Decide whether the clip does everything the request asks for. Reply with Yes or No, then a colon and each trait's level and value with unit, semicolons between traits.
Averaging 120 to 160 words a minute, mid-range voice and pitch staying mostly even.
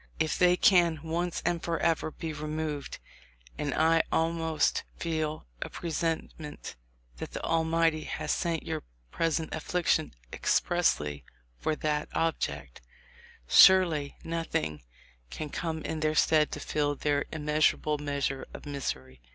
Yes: slow, 135 wpm; medium, 155 Hz; narrow, 1.8 semitones